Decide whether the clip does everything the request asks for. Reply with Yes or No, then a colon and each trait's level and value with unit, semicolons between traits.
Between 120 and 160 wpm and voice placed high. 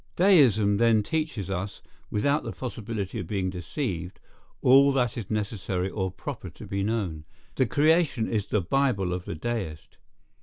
No: average, 155 wpm; low, 105 Hz